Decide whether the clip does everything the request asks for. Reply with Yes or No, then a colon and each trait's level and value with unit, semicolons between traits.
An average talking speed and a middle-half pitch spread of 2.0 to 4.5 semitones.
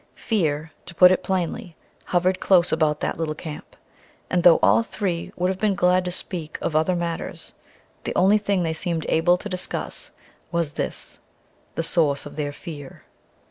Yes: average, 175 wpm; narrow, 2.5 semitones